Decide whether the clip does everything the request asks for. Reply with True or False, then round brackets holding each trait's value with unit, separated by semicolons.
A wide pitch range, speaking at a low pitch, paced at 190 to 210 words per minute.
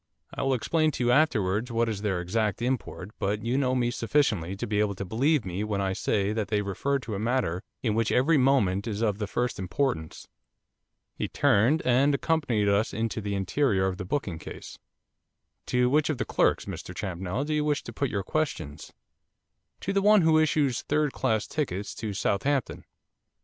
True (5.8 semitones; 115 Hz; 195 wpm)